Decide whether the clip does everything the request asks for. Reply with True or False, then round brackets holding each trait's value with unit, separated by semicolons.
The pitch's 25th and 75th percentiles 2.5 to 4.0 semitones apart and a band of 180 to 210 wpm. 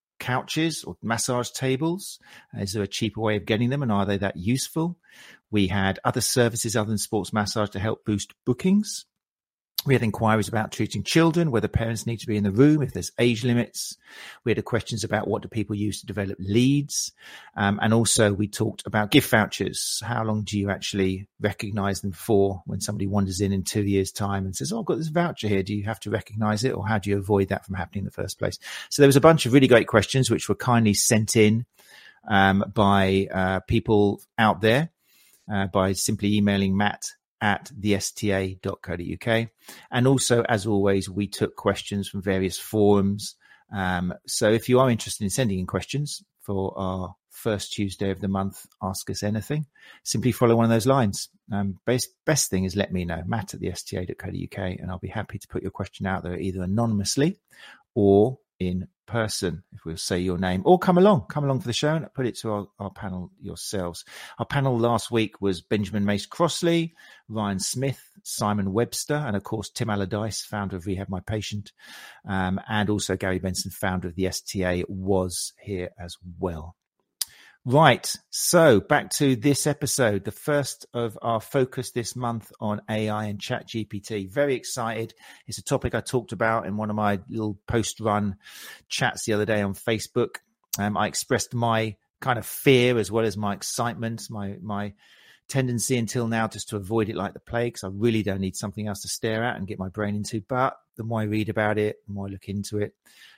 True (3.1 semitones; 200 wpm)